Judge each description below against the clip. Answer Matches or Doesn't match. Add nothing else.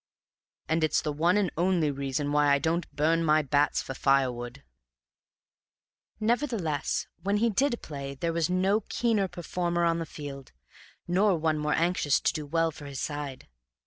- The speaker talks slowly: Doesn't match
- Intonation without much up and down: Doesn't match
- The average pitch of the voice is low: Doesn't match